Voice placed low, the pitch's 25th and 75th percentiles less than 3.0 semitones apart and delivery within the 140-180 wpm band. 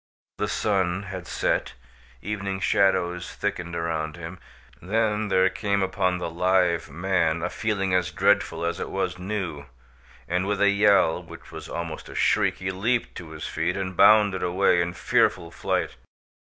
Yes: very low, 95 Hz; narrow, 2.6 semitones; average, 160 wpm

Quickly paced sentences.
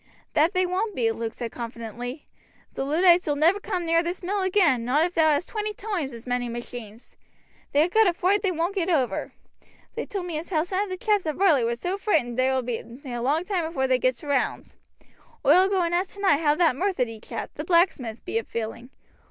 Yes: fast, 225 wpm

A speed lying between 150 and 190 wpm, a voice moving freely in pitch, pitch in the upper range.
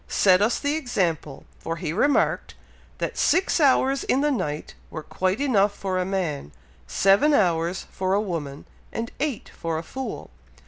Yes: average, 165 wpm; wide, 7.8 semitones; high, 195 Hz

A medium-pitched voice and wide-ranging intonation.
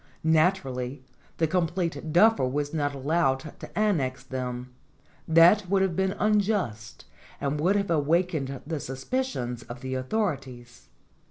Yes: medium, 155 Hz; wide, 6.0 semitones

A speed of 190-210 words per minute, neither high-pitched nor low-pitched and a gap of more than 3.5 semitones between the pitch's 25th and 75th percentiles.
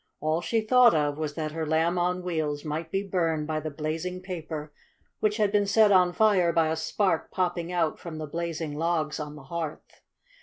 No: average, 200 wpm; medium, 165 Hz; average, 2.8 semitones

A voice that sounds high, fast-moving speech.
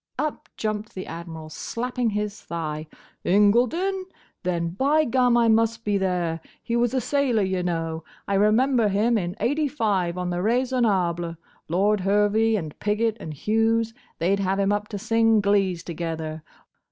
No: high, 205 Hz; average, 155 wpm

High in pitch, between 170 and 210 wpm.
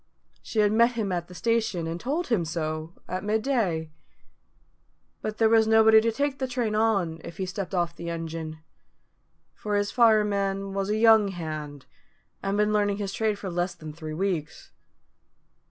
Yes: high, 200 Hz; average, 175 wpm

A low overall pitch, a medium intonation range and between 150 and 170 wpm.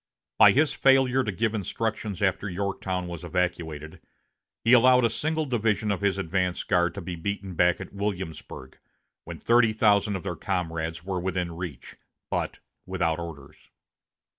Yes: very low, 95 Hz; average, 3.8 semitones; average, 155 wpm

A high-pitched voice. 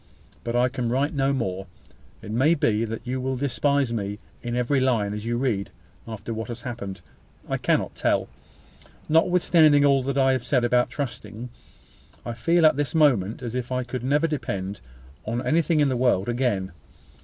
No: low, 125 Hz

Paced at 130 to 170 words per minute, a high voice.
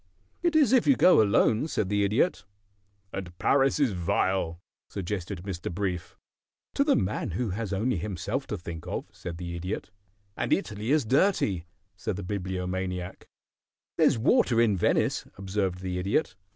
No: average, 155 wpm; low, 100 Hz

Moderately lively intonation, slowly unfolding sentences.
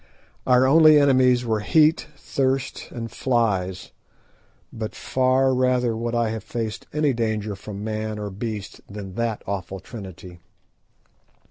Yes: average, 3.6 semitones; slow, 130 wpm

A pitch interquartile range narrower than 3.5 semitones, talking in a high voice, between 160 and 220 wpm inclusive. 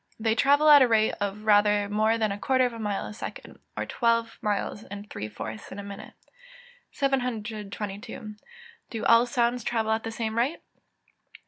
Yes: narrow, 2.4 semitones; high, 220 Hz; average, 190 wpm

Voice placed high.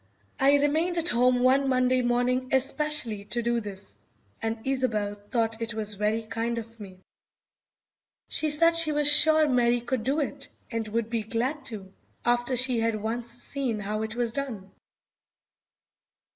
Yes: high, 240 Hz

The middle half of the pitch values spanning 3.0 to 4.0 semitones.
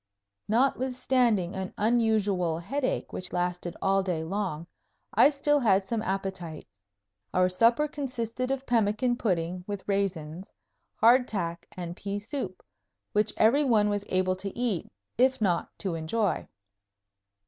No: average, 4.8 semitones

